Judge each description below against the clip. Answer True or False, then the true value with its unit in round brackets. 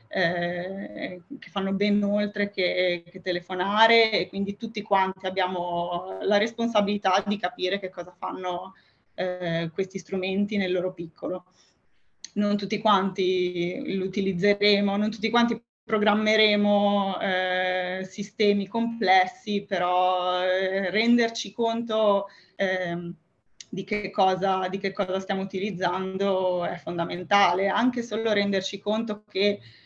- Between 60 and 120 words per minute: True (115 wpm)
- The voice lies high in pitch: True (195 Hz)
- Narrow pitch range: True (2.1 semitones)